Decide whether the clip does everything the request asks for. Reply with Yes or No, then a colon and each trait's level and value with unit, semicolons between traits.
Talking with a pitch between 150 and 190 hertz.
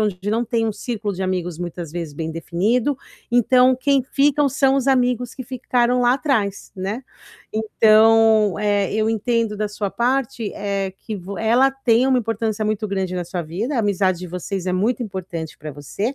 No: high, 215 Hz